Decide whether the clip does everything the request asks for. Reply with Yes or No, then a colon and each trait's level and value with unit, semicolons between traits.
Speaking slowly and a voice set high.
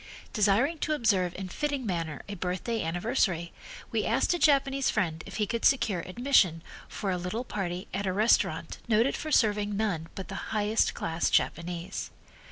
No: average, 170 wpm; high, 205 Hz